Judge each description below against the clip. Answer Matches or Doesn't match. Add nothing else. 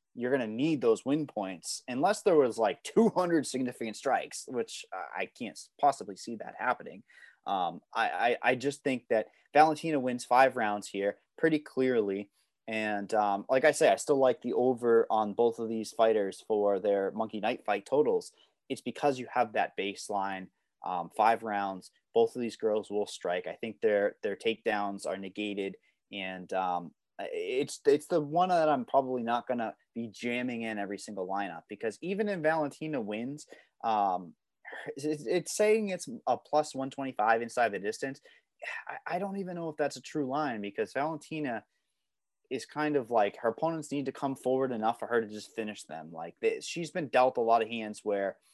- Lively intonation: Matches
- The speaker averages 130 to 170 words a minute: Doesn't match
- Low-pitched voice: Matches